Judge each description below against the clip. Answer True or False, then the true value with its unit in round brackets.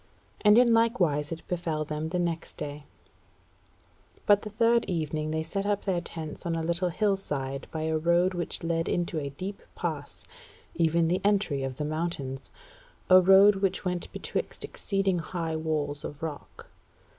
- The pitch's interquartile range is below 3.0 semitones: False (3.8 semitones)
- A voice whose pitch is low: False (170 Hz)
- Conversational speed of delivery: True (165 wpm)